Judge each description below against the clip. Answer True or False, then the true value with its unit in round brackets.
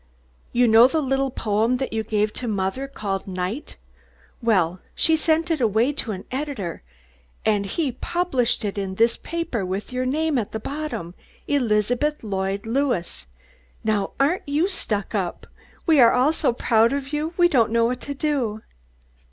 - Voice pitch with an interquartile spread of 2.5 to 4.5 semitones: False (5.4 semitones)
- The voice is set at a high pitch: True (240 Hz)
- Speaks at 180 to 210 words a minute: False (170 wpm)